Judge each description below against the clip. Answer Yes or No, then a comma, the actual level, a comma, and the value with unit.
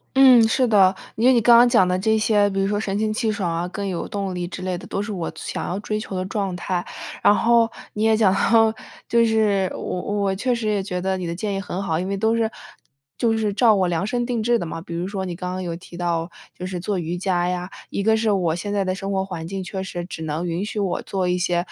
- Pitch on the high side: Yes, high, 195 Hz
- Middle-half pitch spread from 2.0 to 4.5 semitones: Yes, average, 3.2 semitones